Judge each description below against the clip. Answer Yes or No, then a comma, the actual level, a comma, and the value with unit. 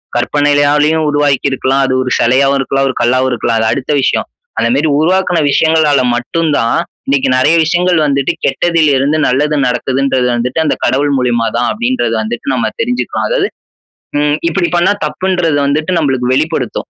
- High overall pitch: No, medium, 140 Hz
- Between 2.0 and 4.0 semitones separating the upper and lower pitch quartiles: Yes, average, 3.7 semitones